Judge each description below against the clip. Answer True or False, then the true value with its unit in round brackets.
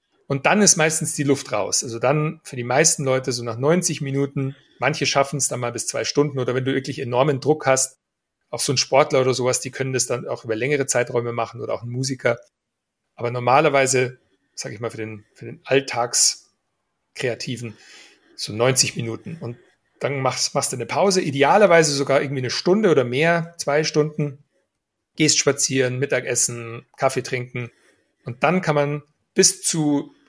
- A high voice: False (135 Hz)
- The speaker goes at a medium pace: True (180 wpm)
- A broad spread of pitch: False (3.3 semitones)